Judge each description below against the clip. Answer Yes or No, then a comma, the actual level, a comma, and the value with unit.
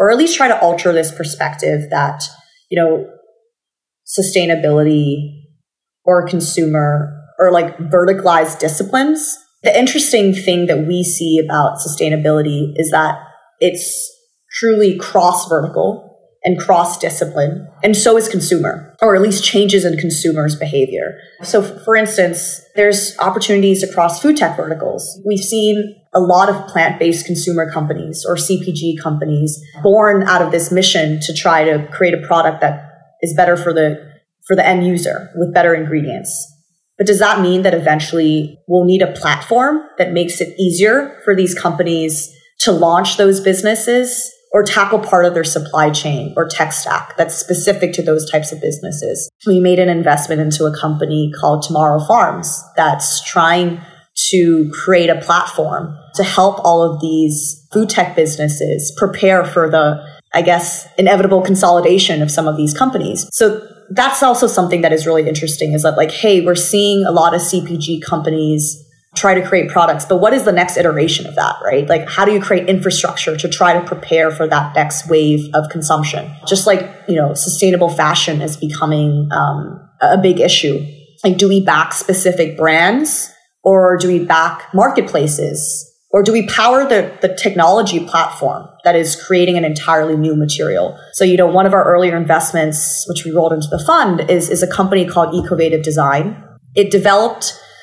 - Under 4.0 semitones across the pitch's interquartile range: Yes, average, 3.4 semitones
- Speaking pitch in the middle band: Yes, medium, 175 Hz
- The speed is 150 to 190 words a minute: Yes, average, 165 wpm